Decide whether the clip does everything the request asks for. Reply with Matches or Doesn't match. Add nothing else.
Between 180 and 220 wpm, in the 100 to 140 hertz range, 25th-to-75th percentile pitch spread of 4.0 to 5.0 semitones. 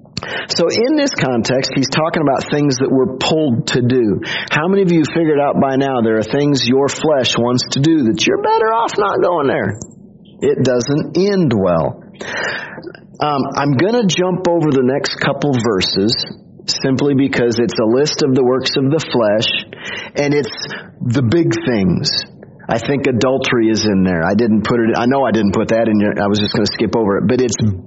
Matches